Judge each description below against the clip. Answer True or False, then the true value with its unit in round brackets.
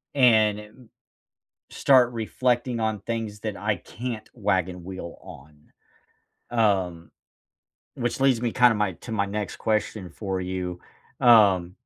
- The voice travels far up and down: False (3.9 semitones)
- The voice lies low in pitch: True (105 Hz)